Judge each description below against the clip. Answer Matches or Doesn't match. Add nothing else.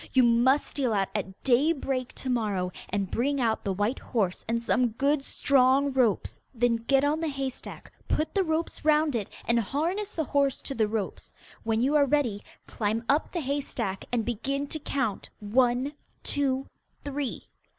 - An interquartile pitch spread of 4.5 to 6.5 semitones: Doesn't match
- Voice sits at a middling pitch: Doesn't match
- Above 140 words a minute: Matches